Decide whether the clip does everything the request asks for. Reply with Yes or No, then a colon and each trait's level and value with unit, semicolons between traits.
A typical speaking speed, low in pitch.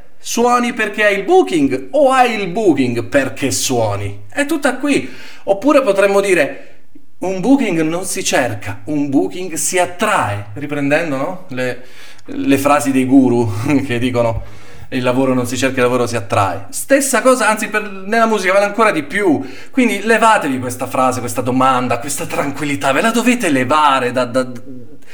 No: average, 160 wpm; medium, 145 Hz